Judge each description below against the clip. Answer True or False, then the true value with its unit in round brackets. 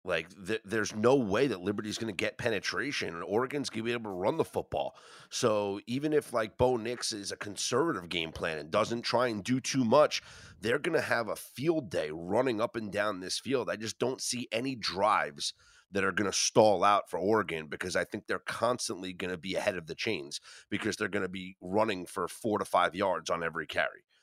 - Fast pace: True (230 wpm)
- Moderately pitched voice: False (110 Hz)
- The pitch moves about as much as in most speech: True (4.4 semitones)